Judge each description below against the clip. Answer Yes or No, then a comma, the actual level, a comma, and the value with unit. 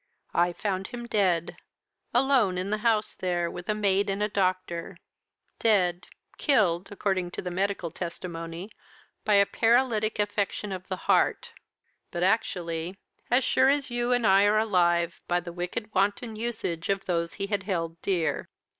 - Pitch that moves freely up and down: No, average, 3.4 semitones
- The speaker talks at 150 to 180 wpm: Yes, average, 160 wpm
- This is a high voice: Yes, high, 195 Hz